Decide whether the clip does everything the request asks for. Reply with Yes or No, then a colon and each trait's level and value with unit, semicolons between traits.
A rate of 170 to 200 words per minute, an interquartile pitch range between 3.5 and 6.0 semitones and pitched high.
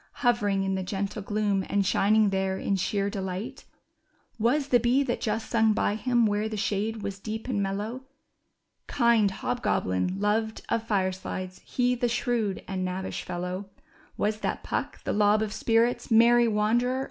No: average, 175 wpm; average, 3.1 semitones; high, 210 Hz